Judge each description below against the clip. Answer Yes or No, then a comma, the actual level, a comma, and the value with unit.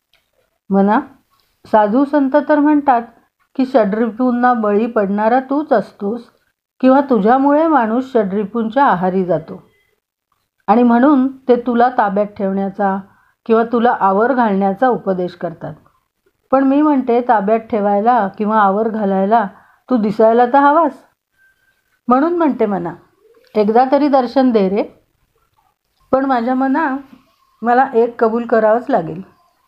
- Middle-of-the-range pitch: No, high, 240 Hz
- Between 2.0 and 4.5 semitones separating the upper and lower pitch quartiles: Yes, average, 4.2 semitones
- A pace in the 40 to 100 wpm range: No, average, 115 wpm